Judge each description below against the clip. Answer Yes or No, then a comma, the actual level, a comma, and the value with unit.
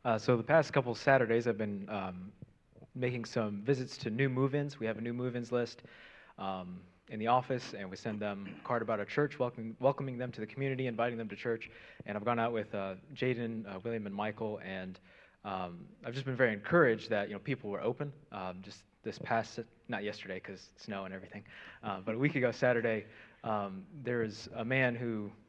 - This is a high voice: No, low, 115 Hz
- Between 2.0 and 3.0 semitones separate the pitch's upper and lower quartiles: No, average, 3.6 semitones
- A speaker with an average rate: No, fast, 210 wpm